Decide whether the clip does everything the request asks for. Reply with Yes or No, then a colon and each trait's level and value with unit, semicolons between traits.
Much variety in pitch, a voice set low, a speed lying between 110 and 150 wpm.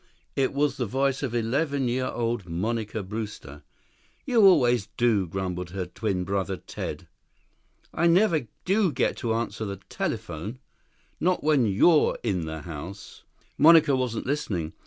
Yes: wide, 6.6 semitones; low, 115 Hz; average, 145 wpm